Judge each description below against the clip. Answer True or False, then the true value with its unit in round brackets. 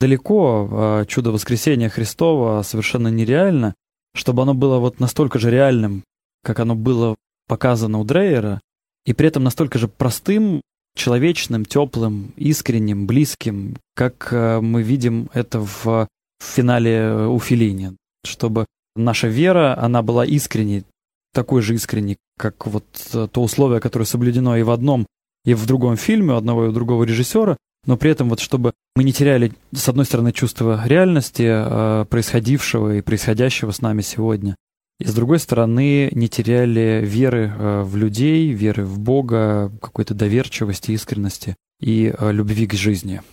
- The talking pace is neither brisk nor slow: True (145 wpm)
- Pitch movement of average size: True (3.1 semitones)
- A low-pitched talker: True (115 Hz)